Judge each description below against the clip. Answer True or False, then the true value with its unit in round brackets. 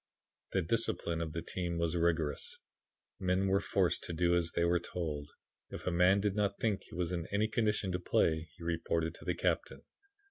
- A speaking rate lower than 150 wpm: False (200 wpm)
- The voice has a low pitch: True (85 Hz)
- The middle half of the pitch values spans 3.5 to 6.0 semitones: False (2.6 semitones)